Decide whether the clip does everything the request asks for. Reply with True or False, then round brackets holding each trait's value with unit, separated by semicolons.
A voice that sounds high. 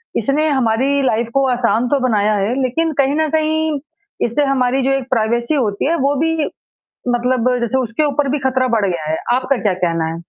True (255 Hz)